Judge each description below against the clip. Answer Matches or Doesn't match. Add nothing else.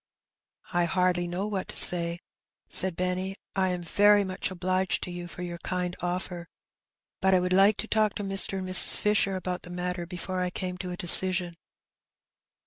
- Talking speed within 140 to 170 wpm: Doesn't match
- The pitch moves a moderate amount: Doesn't match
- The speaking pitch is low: Doesn't match